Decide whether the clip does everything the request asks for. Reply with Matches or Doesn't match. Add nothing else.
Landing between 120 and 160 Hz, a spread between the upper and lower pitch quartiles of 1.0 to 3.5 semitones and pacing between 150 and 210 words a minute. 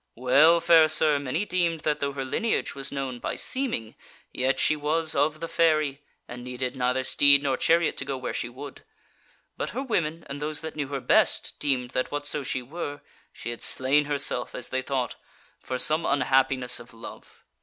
Matches